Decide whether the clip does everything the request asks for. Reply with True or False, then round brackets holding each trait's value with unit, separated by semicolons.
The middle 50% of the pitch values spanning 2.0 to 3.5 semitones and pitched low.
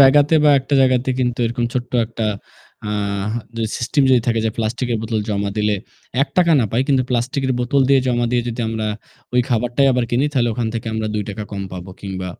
True (2.9 semitones; 120 Hz)